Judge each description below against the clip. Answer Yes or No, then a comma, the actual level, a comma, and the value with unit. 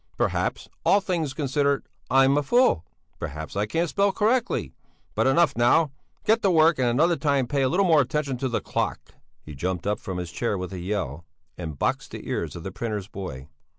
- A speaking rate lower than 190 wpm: No, average, 200 wpm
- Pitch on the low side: Yes, low, 130 Hz